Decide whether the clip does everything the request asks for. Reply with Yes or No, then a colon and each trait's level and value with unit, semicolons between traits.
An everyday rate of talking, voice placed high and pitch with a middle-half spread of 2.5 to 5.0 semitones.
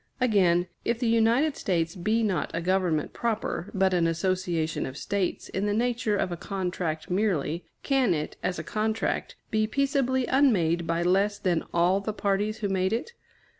Yes: average, 170 wpm; high, 195 Hz; average, 4.3 semitones